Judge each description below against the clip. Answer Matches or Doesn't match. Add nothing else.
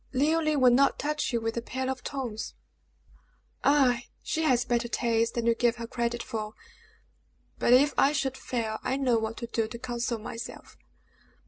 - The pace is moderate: Matches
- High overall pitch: Matches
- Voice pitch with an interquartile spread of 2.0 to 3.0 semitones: Matches